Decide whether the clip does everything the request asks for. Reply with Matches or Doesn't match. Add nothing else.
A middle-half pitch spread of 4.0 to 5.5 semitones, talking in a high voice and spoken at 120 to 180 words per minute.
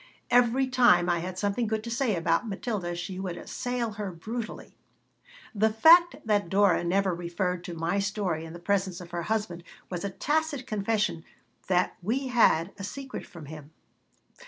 Matches